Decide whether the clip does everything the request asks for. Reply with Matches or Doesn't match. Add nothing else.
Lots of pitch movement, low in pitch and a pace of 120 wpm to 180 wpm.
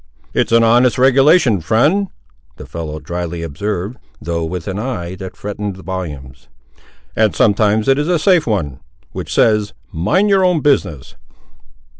Matches